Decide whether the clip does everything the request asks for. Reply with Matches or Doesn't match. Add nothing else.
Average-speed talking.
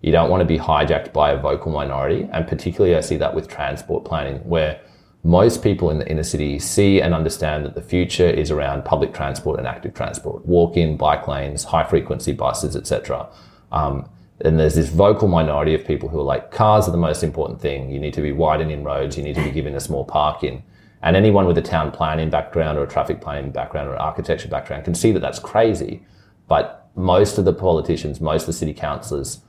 Doesn't match